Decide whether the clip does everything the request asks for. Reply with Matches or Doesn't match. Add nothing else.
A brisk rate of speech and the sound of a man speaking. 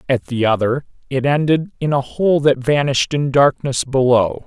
Doesn't match